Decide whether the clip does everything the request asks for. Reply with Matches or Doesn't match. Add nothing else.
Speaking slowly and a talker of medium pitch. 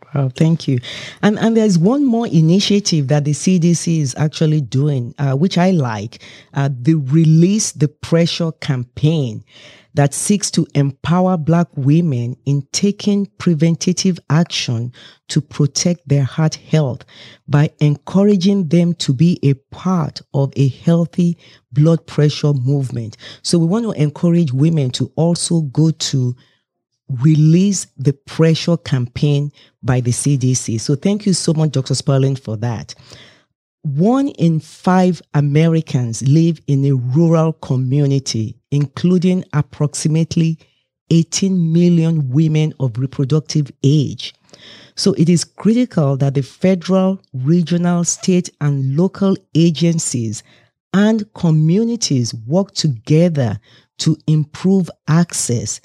Matches